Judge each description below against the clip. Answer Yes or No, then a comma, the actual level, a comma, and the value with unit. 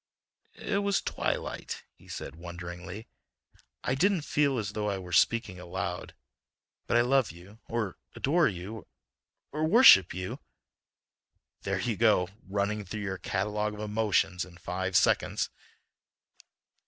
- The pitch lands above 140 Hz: No, low, 105 Hz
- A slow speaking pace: Yes, slow, 125 wpm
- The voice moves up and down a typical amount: Yes, average, 4.1 semitones